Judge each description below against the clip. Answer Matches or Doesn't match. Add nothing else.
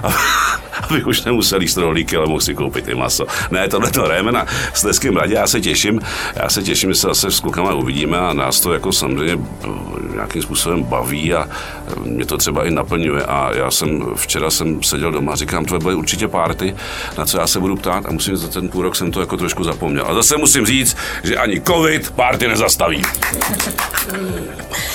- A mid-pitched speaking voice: Doesn't match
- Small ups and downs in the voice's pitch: Doesn't match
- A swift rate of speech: Matches